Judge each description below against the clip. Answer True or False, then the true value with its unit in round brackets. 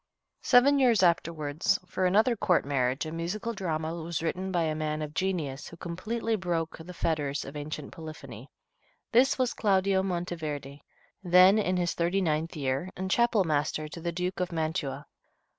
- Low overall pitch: False (170 Hz)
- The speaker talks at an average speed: True (165 wpm)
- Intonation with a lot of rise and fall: False (3.6 semitones)